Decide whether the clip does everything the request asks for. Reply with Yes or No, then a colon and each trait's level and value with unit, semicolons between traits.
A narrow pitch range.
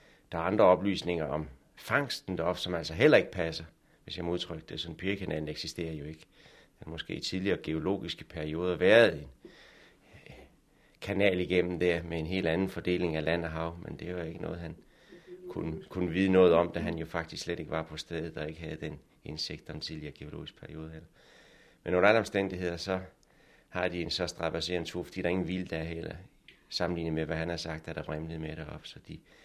Yes: narrow, 2.0 semitones